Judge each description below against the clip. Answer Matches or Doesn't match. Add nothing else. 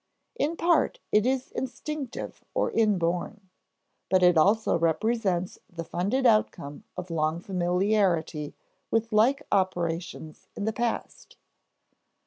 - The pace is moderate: Doesn't match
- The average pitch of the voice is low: Doesn't match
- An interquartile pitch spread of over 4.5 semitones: Matches